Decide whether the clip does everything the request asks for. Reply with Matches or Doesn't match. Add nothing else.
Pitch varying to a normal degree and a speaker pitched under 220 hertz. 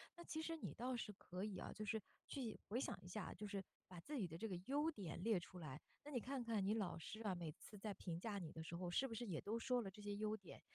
Matches